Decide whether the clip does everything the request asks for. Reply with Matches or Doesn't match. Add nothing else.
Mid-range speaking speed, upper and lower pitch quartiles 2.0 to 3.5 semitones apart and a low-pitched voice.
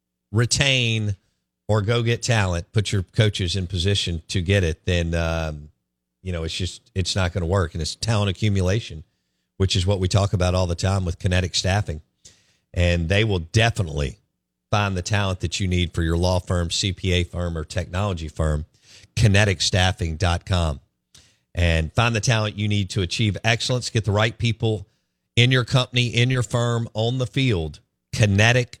Doesn't match